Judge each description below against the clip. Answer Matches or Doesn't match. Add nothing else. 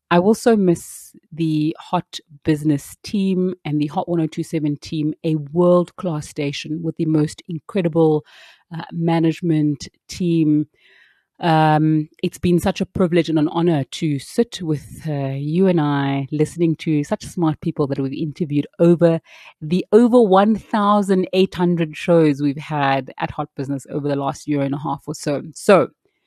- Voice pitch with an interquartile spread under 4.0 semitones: Matches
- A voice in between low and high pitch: Matches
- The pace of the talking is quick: Doesn't match